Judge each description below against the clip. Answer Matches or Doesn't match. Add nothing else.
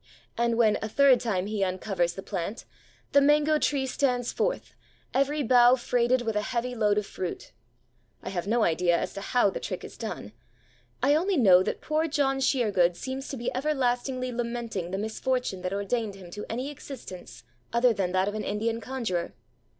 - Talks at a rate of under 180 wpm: Doesn't match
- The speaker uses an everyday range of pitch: Matches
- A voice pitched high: Matches